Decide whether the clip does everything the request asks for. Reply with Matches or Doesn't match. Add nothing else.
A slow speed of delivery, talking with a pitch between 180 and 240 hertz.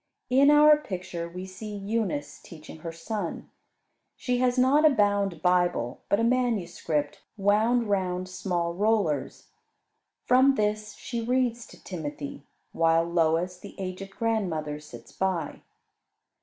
Matches